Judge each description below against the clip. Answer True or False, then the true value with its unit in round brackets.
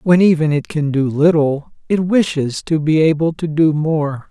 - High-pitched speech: False (155 Hz)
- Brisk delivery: False (195 wpm)